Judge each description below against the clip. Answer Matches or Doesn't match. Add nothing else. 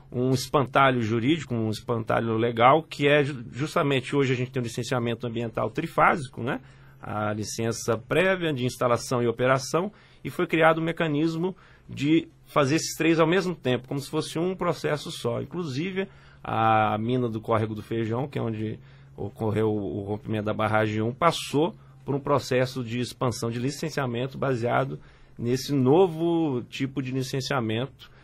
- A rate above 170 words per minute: Doesn't match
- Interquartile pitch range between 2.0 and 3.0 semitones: Doesn't match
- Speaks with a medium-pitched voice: Doesn't match